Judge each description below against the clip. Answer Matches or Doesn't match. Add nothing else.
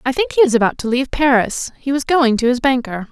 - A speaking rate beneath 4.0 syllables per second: Doesn't match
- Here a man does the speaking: Doesn't match